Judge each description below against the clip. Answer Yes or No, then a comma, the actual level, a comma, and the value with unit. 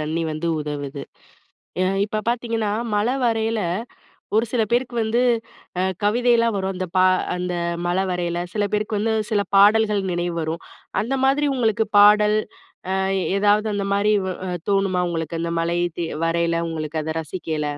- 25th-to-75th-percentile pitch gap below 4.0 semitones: No, average, 4.6 semitones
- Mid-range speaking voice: No, high, 200 Hz